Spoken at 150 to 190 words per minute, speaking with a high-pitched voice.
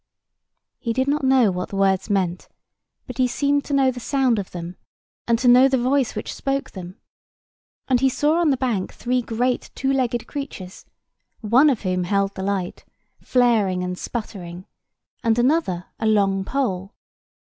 Yes: average, 170 wpm; high, 235 Hz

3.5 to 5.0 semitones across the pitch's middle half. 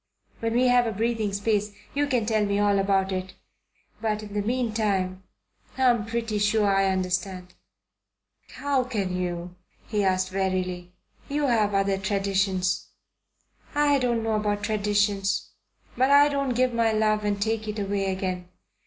No: average, 2.9 semitones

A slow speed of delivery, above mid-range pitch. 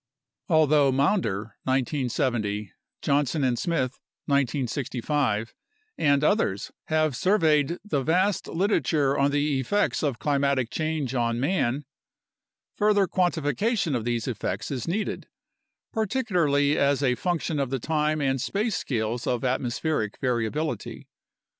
No: slow, 120 wpm; medium, 140 Hz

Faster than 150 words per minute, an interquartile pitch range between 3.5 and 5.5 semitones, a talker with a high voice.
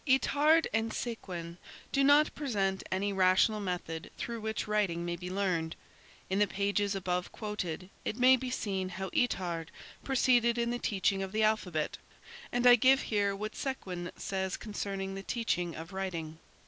Yes: average, 160 wpm; average, 4.2 semitones; high, 200 Hz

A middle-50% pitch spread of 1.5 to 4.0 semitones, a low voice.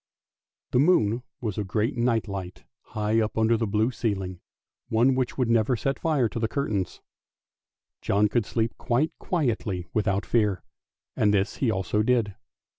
Yes: average, 2.9 semitones; low, 110 Hz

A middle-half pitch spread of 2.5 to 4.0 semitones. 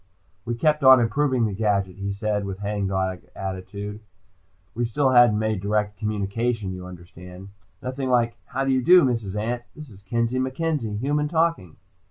No: average, 4.6 semitones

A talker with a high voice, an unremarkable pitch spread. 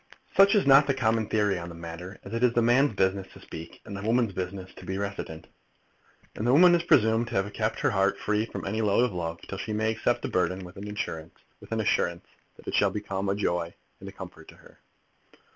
No: low, 105 Hz; average, 3.8 semitones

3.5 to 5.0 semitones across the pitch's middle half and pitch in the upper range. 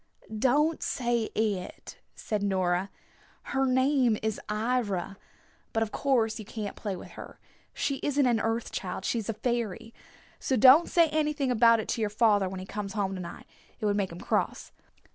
Yes: average, 3.9 semitones; high, 225 Hz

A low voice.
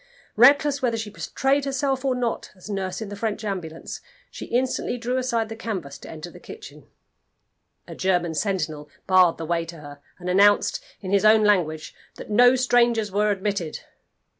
No: high, 205 Hz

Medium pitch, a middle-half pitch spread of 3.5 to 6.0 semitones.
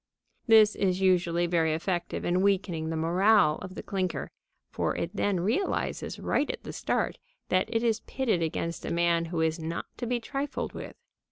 Yes: medium, 180 Hz; average, 3.8 semitones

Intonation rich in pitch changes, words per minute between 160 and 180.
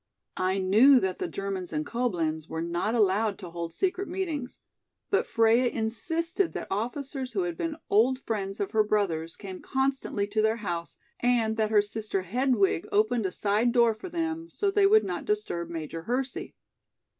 Yes: wide, 5.7 semitones; average, 175 wpm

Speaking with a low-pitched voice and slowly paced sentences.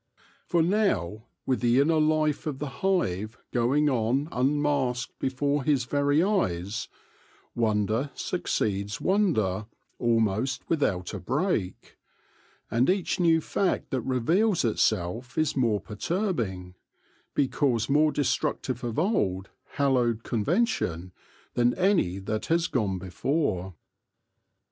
Yes: low, 130 Hz; slow, 115 wpm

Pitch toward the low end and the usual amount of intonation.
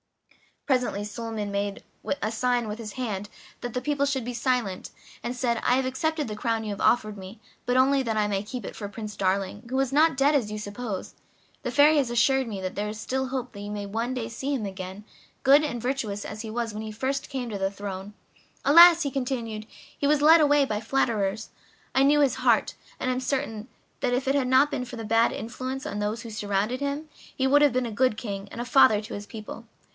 No: high, 235 Hz; average, 4.0 semitones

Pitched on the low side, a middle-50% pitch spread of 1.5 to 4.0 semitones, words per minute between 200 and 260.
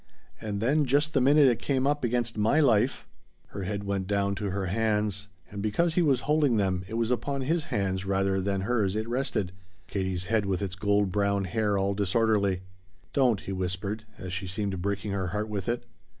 Yes: low, 105 Hz; average, 3.7 semitones; fast, 205 wpm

